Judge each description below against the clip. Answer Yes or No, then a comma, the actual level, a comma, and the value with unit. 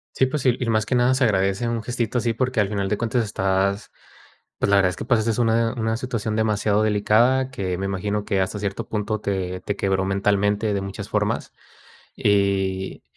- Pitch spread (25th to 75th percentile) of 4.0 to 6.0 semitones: No, average, 2.9 semitones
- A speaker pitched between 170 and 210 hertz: No, low, 105 Hz